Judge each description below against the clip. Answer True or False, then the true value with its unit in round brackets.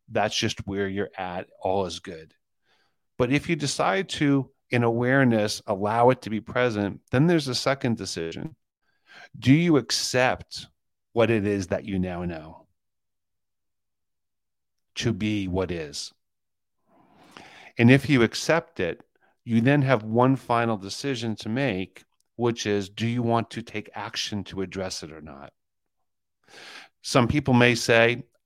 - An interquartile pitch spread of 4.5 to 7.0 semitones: True (4.8 semitones)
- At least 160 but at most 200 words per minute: False (145 wpm)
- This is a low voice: True (110 Hz)